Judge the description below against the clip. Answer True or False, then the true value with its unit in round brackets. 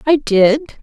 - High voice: True (260 Hz)